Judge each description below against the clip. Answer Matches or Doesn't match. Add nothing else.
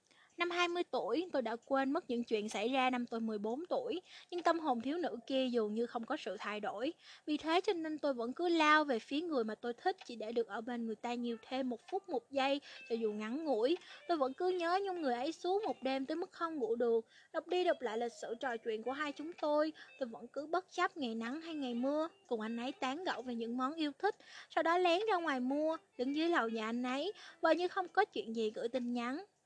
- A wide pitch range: Matches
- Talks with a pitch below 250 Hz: Doesn't match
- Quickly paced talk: Matches